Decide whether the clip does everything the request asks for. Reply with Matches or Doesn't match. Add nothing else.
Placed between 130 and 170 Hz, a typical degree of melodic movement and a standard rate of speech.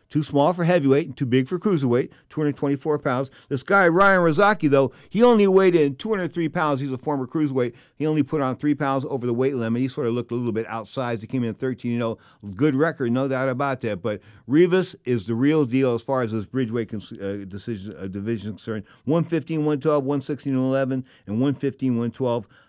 Doesn't match